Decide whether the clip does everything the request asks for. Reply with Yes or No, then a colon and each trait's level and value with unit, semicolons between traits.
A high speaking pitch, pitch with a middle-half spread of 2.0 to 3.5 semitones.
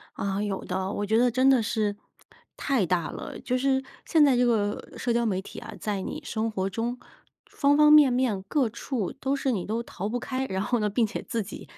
No: high, 230 Hz; average, 4.1 semitones